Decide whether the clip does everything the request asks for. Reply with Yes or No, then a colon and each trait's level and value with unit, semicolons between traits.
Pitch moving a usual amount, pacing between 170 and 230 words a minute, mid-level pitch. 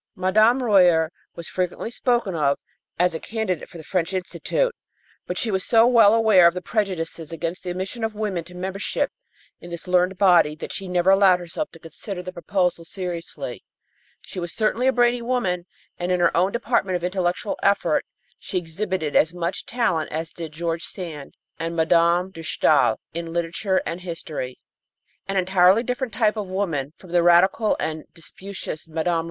Yes: average, 3.1 semitones; average, 175 wpm; medium, 180 Hz